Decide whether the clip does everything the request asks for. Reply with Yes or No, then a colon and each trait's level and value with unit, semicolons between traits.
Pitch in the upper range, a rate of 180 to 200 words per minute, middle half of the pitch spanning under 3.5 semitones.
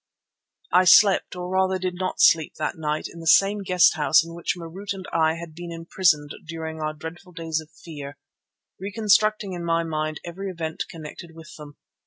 No: medium, 170 Hz; average, 185 wpm; average, 2.7 semitones